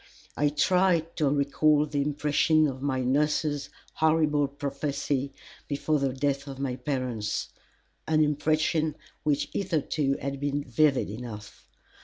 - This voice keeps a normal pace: No, slow, 125 wpm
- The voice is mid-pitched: Yes, medium, 145 Hz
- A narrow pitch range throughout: Yes, narrow, 1.9 semitones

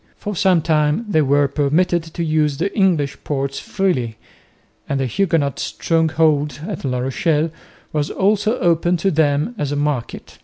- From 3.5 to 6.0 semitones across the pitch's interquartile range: Yes, average, 3.8 semitones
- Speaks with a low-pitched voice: No, medium, 155 Hz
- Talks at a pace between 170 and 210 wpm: No, average, 155 wpm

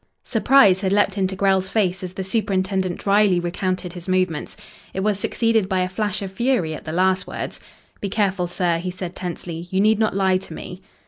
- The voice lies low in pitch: No, high, 190 Hz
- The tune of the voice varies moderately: No, narrow, 1.8 semitones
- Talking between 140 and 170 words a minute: No, average, 200 wpm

